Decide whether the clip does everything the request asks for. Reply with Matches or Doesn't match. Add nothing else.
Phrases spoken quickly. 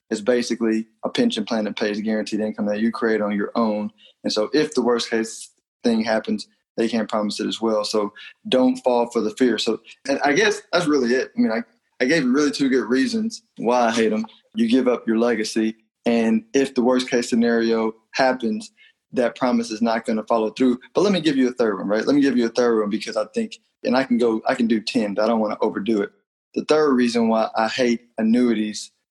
Matches